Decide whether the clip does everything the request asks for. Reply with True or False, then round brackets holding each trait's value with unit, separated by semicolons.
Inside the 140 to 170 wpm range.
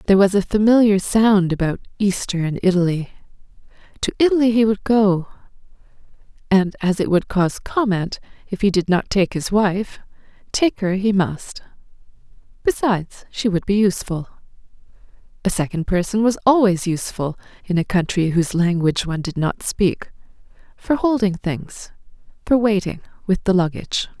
True (145 wpm)